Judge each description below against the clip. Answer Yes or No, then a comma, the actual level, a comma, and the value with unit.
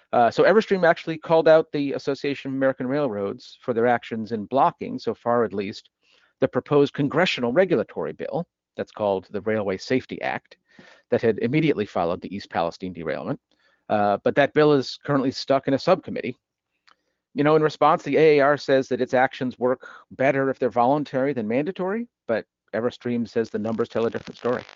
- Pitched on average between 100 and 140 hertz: Yes, low, 135 Hz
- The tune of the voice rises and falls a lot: No, average, 4.1 semitones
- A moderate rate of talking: Yes, average, 180 wpm